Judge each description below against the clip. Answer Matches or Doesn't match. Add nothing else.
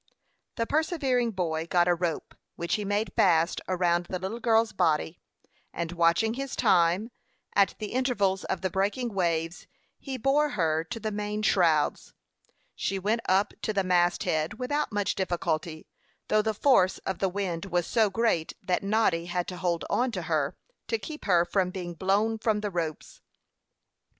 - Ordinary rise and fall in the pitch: Matches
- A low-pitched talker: Doesn't match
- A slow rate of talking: Doesn't match